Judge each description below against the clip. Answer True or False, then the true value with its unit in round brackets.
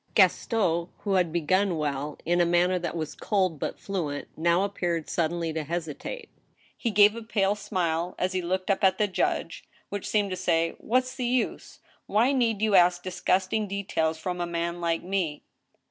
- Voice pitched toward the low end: False (180 Hz)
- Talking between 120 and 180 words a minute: False (190 wpm)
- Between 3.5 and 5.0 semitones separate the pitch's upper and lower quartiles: False (3.1 semitones)